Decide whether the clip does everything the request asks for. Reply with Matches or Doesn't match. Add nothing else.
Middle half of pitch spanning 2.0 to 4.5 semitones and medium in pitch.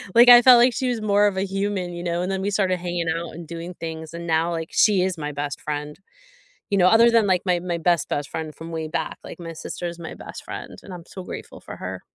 Matches